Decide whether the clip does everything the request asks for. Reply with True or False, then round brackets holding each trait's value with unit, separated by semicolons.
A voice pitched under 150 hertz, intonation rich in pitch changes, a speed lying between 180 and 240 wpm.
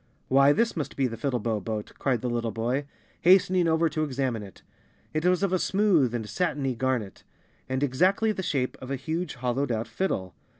True (135 Hz; 6.0 semitones; 200 wpm)